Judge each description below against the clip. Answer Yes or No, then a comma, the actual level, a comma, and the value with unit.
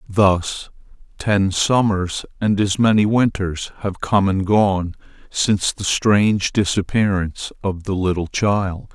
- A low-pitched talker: Yes, low, 100 Hz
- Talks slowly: Yes, slow, 125 wpm